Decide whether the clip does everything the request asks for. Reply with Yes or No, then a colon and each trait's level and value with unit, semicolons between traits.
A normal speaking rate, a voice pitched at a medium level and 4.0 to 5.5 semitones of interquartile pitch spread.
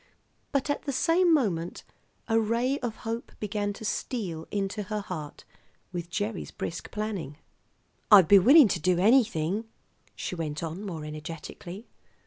No: average, 145 wpm; high, 205 Hz; average, 5.0 semitones